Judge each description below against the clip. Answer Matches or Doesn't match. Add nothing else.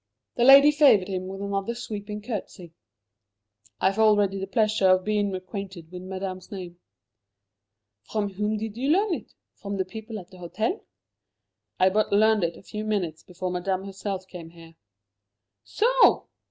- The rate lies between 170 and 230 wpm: Doesn't match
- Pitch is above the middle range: Matches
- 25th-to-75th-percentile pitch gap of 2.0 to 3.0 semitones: Matches